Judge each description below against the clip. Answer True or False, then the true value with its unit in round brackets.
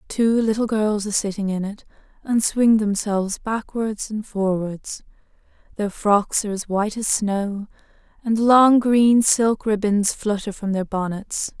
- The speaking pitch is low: False (210 Hz)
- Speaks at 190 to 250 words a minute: False (150 wpm)